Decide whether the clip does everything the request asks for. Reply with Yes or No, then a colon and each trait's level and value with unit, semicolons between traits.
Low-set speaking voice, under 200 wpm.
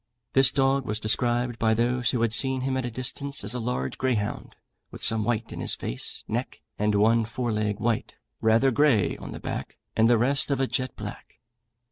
No: low, 120 Hz; fast, 205 wpm